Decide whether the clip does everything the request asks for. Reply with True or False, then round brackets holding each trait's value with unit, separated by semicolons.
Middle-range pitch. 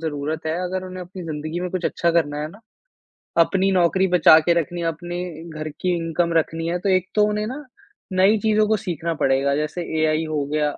True (170 Hz)